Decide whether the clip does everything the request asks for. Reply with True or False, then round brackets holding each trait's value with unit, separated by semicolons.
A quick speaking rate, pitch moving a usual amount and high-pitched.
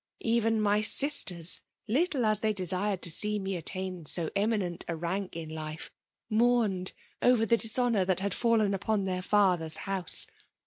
False (165 wpm; 3.5 semitones; 200 Hz)